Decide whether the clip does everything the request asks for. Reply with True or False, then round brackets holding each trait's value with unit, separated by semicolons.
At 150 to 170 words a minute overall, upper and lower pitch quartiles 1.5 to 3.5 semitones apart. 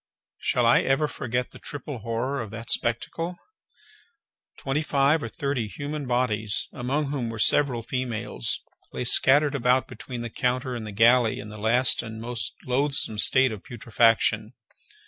True (155 wpm; 3.1 semitones)